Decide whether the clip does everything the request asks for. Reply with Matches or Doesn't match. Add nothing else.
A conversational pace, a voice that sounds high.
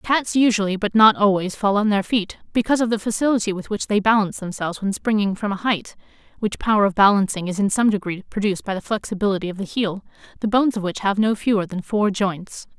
Doesn't match